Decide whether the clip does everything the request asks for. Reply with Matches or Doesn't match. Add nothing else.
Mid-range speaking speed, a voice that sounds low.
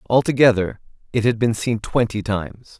Matches